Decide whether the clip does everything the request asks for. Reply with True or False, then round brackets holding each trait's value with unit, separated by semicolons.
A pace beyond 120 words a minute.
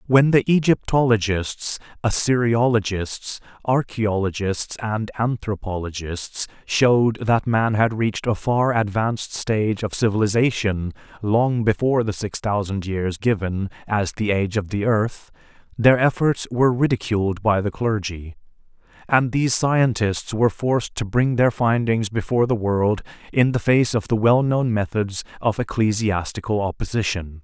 True (135 wpm)